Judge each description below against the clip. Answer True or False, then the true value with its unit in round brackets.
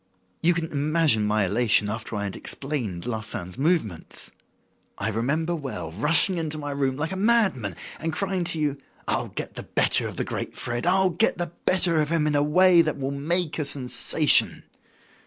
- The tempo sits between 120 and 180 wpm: False (190 wpm)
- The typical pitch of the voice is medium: True (150 Hz)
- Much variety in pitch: True (5.9 semitones)